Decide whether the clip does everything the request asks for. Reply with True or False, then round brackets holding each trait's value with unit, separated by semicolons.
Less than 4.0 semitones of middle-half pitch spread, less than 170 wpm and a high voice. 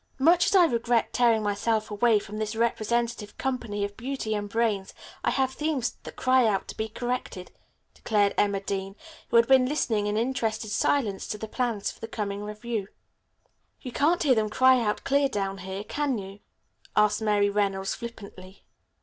False (3.4 semitones; 175 wpm; 220 Hz)